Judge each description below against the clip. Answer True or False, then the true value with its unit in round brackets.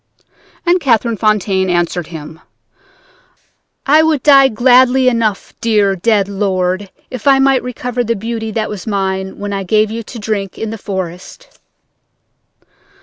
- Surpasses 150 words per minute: False (145 wpm)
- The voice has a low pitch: False (215 Hz)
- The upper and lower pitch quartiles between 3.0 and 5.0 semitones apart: True (4.3 semitones)